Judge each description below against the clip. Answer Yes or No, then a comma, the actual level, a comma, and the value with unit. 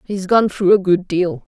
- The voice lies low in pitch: No, high, 190 Hz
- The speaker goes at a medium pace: No, fast, 230 wpm